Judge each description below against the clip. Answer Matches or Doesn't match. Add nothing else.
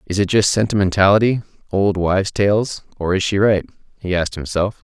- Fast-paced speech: Doesn't match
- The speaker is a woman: Doesn't match